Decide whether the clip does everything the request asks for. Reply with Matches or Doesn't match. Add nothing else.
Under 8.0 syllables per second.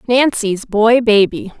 Matches